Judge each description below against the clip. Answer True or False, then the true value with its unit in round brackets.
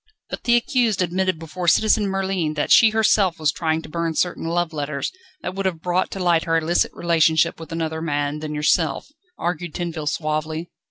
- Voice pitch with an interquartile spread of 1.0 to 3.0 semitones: True (2.7 semitones)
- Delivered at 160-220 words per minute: True (185 wpm)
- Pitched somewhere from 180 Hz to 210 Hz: False (170 Hz)